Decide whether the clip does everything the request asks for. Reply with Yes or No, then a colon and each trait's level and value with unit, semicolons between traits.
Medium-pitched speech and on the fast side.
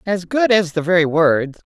Yes: medium, 175 Hz; fast, 210 wpm